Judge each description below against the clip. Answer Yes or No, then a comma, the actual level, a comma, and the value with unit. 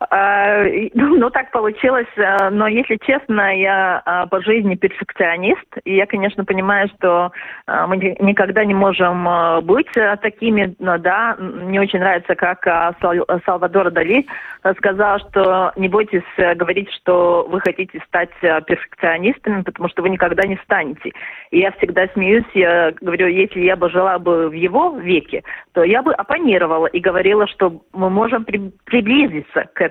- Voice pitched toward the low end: No, high, 190 Hz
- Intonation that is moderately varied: No, narrow, 2.3 semitones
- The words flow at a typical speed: Yes, average, 140 wpm